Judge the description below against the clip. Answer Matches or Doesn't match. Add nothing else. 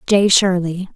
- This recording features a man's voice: Doesn't match